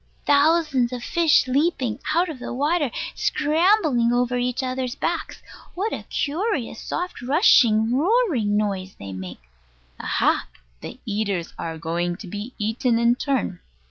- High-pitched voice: Yes, very high, 250 Hz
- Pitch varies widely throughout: Yes, wide, 6.3 semitones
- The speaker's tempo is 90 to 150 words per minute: Yes, average, 140 wpm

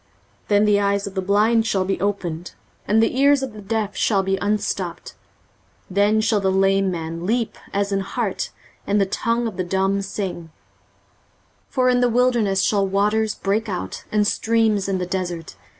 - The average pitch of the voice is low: No, high, 200 Hz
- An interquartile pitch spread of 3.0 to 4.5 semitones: No, narrow, 2.4 semitones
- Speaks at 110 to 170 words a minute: No, average, 185 wpm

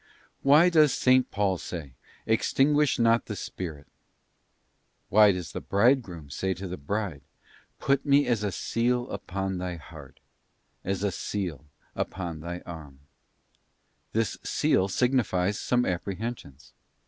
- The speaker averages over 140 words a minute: No, slow, 135 wpm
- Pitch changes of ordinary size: No, wide, 5.7 semitones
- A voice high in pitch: No, low, 100 Hz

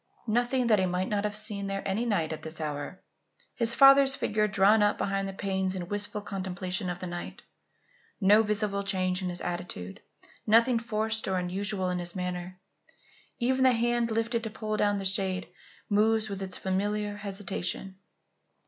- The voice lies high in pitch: Yes, high, 200 Hz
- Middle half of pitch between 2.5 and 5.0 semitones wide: Yes, average, 2.8 semitones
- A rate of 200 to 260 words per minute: No, average, 175 wpm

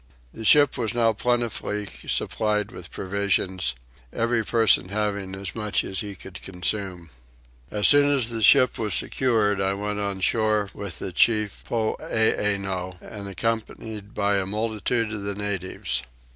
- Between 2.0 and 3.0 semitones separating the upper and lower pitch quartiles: Yes, narrow, 2.5 semitones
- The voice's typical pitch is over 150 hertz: No, low, 105 Hz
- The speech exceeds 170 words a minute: No, average, 145 wpm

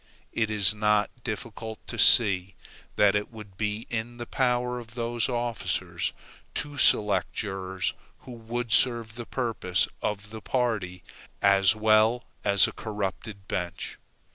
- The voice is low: Yes, low, 110 Hz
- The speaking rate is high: No, average, 140 wpm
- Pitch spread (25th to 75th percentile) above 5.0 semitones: No, average, 3.0 semitones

